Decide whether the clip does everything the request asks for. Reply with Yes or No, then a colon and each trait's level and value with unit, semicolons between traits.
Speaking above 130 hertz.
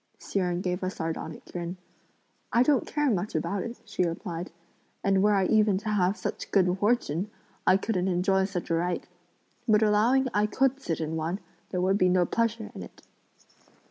Yes: high, 190 Hz